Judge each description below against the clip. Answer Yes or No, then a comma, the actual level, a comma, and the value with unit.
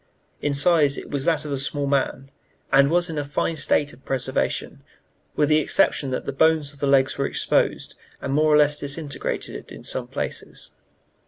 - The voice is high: No, medium, 145 Hz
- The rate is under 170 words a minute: No, average, 190 wpm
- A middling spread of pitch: No, narrow, 1.8 semitones